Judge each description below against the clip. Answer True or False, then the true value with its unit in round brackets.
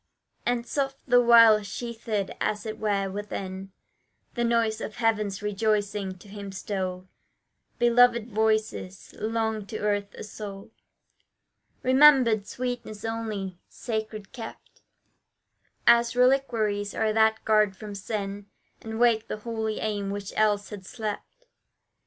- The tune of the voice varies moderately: False (2.3 semitones)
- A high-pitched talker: True (215 Hz)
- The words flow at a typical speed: False (120 wpm)